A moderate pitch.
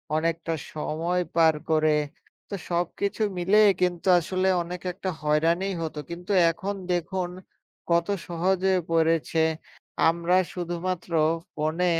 Yes: medium, 170 Hz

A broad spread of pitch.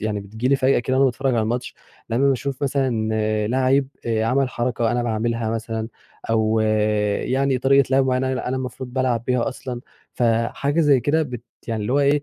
No: average, 2.8 semitones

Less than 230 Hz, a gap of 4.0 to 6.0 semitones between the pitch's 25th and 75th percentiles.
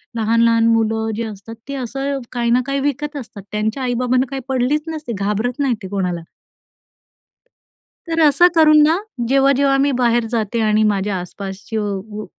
No: high, 235 Hz; average, 4.3 semitones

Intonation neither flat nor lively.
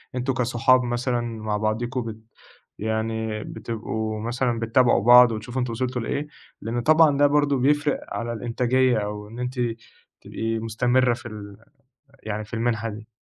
No: narrow, 2.3 semitones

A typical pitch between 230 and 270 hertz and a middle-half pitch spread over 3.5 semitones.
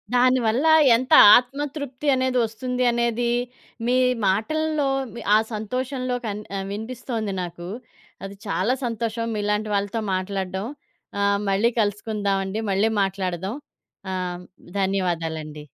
No: high, 215 Hz; average, 4.3 semitones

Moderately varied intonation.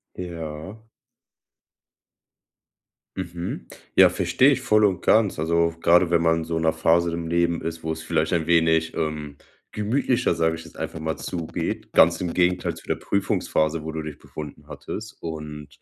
No: narrow, 1.8 semitones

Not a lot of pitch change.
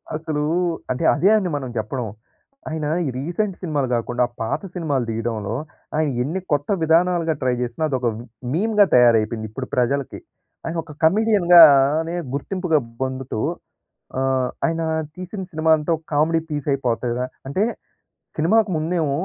No: average, 4.7 semitones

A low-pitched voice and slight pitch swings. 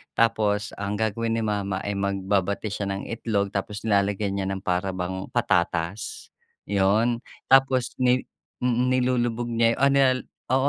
No: low, 105 Hz; average, 3.3 semitones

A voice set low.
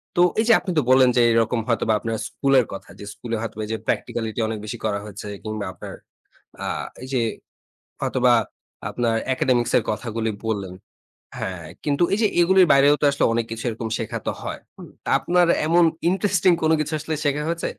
Yes: low, 120 Hz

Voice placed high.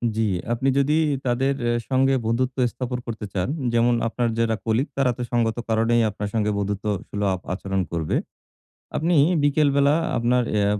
No: low, 120 Hz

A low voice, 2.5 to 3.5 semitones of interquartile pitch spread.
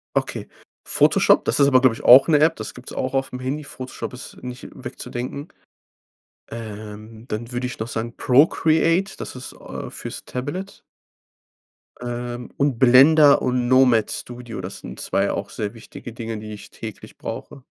Yes: low, 125 Hz; average, 2.9 semitones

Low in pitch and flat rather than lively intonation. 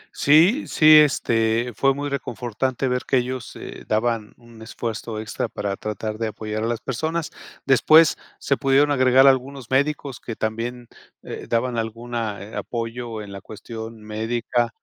No: low, 120 Hz; average, 3.2 semitones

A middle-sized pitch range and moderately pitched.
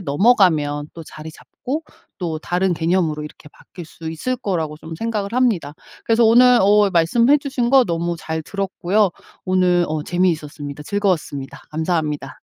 Yes: average, 5.0 semitones; medium, 175 Hz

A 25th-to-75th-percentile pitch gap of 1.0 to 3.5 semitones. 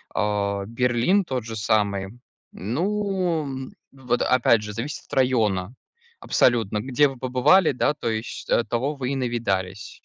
No: average, 4.1 semitones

